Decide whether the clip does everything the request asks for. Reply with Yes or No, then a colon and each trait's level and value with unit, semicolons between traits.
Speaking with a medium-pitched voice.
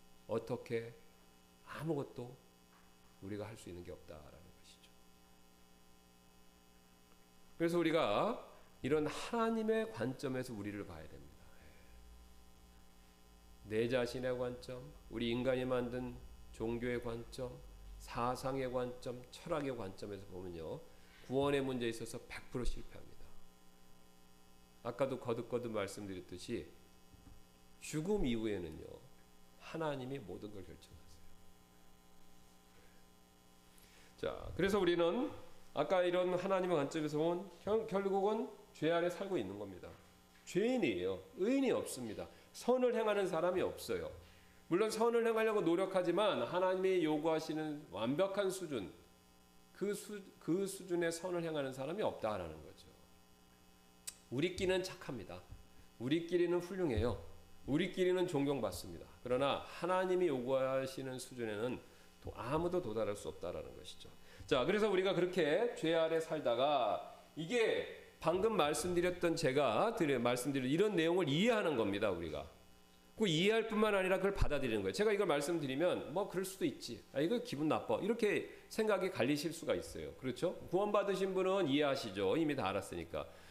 No: low, 125 Hz